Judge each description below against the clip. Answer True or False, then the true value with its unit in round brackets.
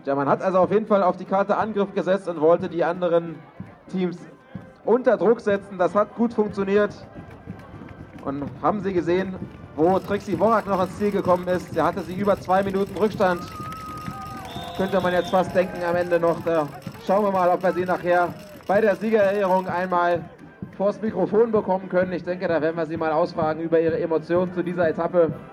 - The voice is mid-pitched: True (180 Hz)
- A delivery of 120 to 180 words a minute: False (190 wpm)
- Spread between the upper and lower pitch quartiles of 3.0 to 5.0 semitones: False (2.4 semitones)